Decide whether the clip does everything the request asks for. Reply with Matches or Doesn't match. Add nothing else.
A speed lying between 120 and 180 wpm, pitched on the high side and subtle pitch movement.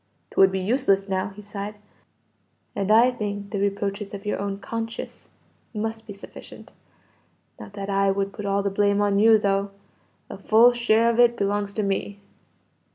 Matches